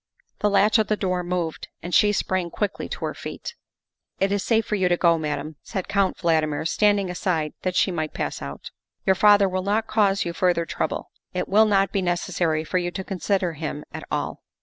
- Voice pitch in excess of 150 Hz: Yes, medium, 185 Hz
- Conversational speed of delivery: No, fast, 215 wpm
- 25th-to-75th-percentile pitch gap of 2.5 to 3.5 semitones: Yes, average, 3.1 semitones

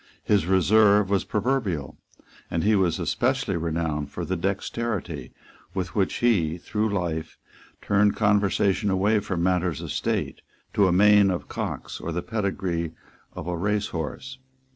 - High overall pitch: No, very low, 95 Hz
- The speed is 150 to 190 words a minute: No, average, 140 wpm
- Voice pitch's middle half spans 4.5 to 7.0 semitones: No, average, 3.6 semitones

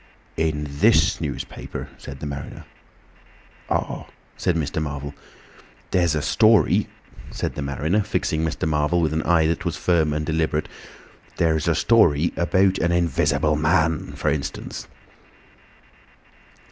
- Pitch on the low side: Yes, very low, 80 Hz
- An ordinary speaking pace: No, slow, 130 wpm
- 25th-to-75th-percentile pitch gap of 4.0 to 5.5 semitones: No, narrow, 2.5 semitones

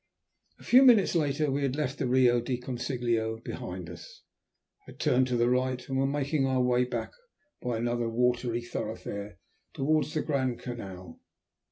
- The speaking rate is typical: Yes, average, 165 wpm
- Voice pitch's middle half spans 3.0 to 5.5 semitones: No, narrow, 2.4 semitones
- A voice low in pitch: Yes, low, 125 Hz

